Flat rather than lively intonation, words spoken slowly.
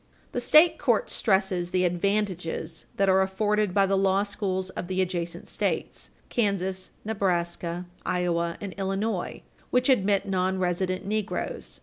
Yes: narrow, 2.2 semitones; slow, 130 wpm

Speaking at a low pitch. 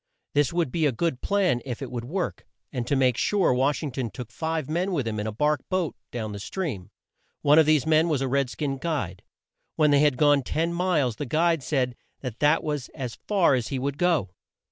No: medium, 145 Hz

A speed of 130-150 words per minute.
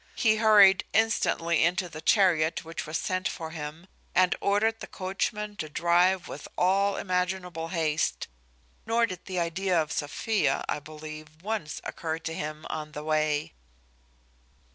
Yes: average, 145 wpm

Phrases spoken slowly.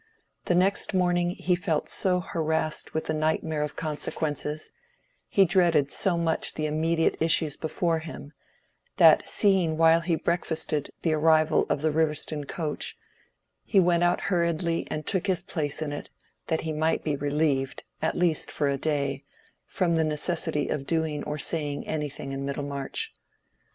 No: average, 150 wpm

